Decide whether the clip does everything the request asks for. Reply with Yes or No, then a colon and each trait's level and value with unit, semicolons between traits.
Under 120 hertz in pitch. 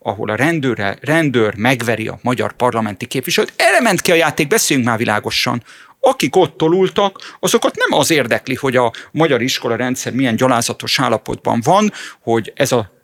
No: low, 130 Hz